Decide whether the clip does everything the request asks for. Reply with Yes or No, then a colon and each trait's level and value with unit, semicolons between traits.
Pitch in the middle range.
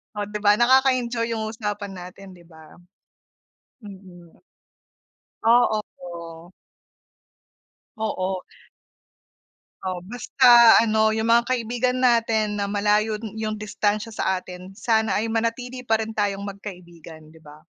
No: high, 210 Hz